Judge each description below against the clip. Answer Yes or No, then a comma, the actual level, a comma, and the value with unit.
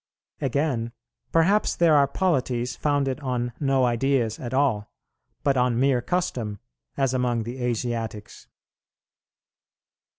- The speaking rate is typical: No, slow, 110 wpm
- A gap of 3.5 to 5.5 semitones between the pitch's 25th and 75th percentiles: No, average, 2.9 semitones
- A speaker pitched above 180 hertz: No, low, 125 Hz